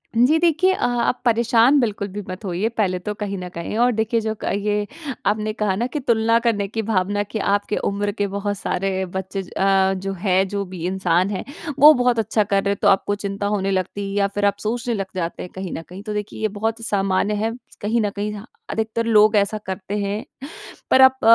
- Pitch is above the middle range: Yes, high, 205 Hz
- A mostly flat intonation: Yes, narrow, 2.3 semitones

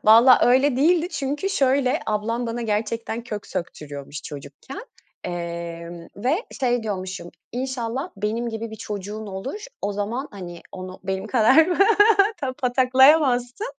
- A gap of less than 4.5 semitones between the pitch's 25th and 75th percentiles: No, average, 5.3 semitones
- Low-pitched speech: No, high, 230 Hz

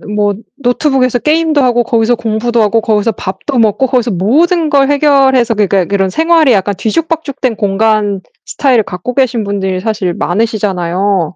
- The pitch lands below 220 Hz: No, high, 225 Hz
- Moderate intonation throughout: Yes, average, 4.8 semitones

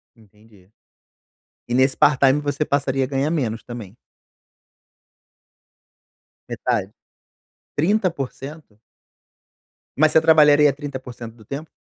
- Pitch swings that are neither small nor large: Yes, average, 3.8 semitones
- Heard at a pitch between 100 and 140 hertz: Yes, low, 135 Hz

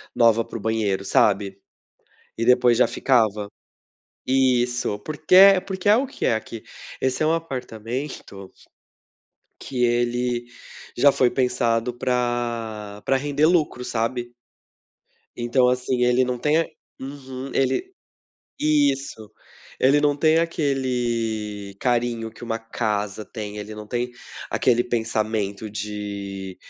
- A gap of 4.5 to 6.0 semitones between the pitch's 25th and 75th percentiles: No, average, 3.4 semitones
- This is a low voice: Yes, low, 120 Hz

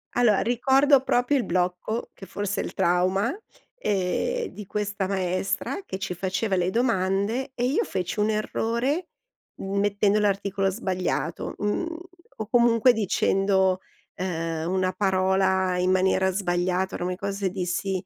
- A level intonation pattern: No, average, 3.3 semitones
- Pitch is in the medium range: No, high, 195 Hz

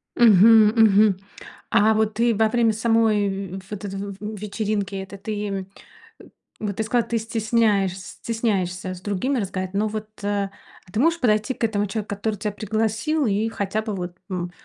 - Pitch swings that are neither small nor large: No, narrow, 2.2 semitones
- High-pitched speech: Yes, high, 210 Hz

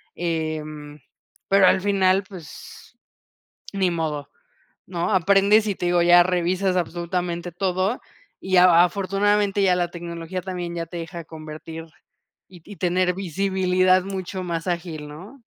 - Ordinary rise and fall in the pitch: No, narrow, 2.1 semitones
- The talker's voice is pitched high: No, medium, 180 Hz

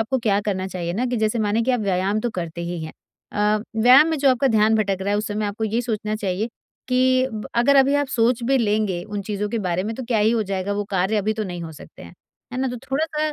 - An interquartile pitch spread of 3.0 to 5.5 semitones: Yes, average, 3.6 semitones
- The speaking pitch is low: No, high, 215 Hz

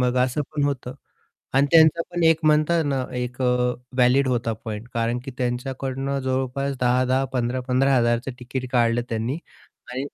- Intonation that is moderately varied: No, narrow, 1.9 semitones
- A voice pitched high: No, low, 130 Hz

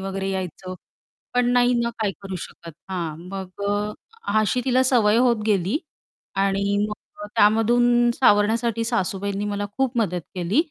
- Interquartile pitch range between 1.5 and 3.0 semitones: No, average, 3.6 semitones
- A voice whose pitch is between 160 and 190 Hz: No, high, 210 Hz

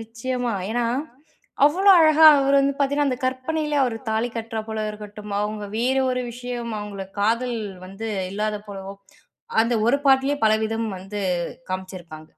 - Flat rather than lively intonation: No, average, 3.8 semitones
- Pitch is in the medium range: No, high, 230 Hz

